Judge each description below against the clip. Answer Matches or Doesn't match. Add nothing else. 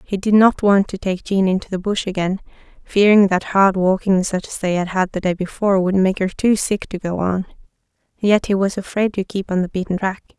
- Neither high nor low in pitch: Doesn't match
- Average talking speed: Doesn't match